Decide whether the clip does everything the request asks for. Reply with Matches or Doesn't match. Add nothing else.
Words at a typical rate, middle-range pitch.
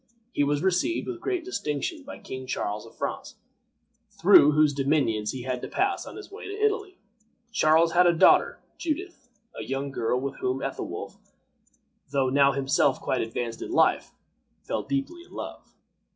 Matches